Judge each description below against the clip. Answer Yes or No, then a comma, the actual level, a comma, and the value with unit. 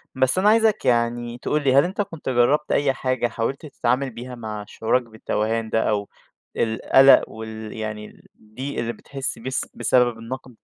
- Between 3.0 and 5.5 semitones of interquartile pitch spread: Yes, average, 3.3 semitones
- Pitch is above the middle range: No, low, 120 Hz